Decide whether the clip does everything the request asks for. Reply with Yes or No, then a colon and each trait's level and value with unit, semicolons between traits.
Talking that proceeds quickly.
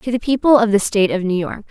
Yes: fast, 315 wpm